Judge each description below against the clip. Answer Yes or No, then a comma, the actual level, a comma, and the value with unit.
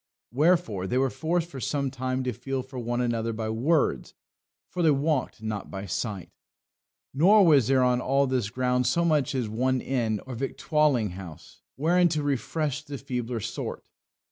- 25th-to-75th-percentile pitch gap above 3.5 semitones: Yes, average, 4.0 semitones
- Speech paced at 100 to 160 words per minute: No, average, 170 wpm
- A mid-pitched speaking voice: No, low, 130 Hz